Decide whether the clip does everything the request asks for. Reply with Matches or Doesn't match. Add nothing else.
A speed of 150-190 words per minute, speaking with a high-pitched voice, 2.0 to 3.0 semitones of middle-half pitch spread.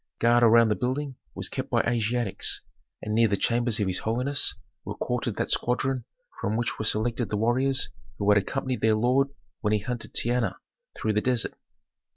Doesn't match